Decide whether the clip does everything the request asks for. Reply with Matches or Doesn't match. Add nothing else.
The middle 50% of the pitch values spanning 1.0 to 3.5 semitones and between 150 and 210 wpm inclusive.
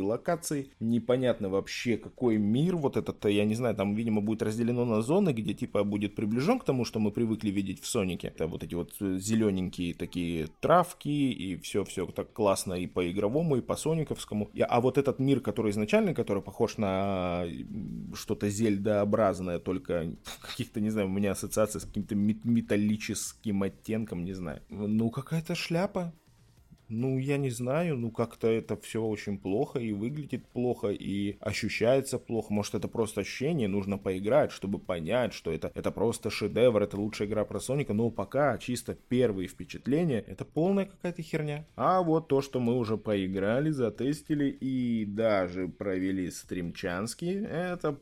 Doesn't match